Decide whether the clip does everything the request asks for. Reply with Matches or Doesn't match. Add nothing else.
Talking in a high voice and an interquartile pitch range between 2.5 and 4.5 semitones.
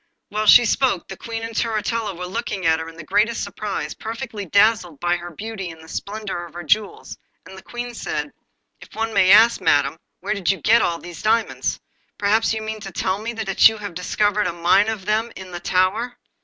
Matches